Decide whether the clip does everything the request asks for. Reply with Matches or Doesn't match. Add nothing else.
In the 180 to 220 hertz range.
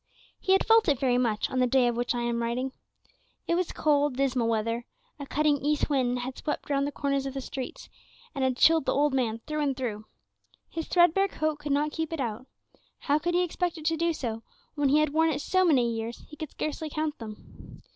Doesn't match